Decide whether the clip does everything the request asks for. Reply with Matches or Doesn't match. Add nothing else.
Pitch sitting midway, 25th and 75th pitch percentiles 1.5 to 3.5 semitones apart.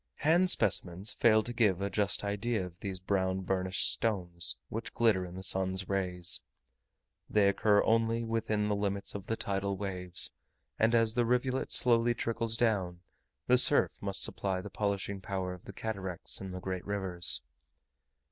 Doesn't match